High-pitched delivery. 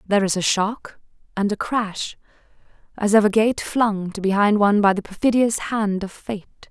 Yes: high, 205 Hz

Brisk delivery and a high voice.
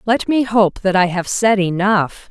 Yes: fast, 210 wpm; high, 200 Hz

